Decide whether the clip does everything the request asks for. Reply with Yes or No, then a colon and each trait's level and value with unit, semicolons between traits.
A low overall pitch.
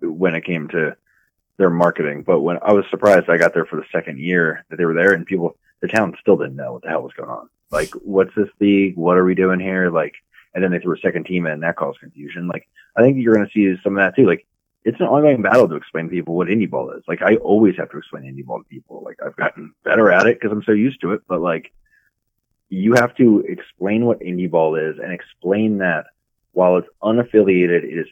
Yes: very low, 90 Hz